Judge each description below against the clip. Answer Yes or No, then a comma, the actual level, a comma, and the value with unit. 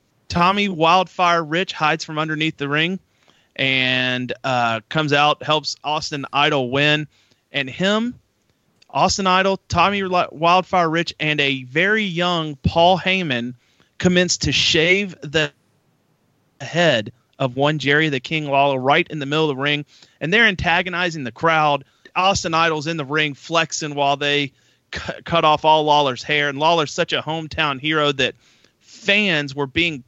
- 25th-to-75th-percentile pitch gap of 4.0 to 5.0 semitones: No, average, 3.1 semitones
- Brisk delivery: No, average, 155 wpm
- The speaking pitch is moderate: Yes, medium, 155 Hz